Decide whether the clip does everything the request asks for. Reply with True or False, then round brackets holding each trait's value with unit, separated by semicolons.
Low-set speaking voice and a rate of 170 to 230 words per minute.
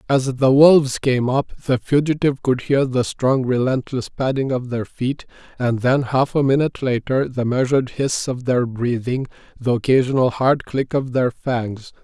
True (130 Hz; 175 wpm)